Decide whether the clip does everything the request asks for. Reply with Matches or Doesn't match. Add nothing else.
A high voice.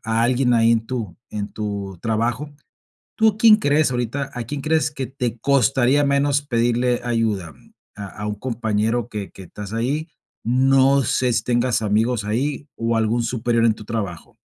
Doesn't match